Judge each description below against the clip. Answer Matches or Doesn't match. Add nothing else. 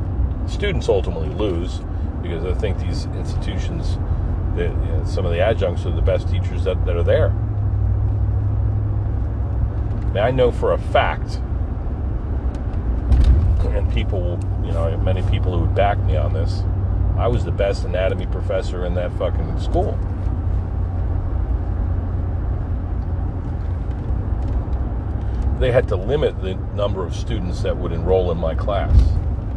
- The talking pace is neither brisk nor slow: Doesn't match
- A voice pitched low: Matches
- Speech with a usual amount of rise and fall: Doesn't match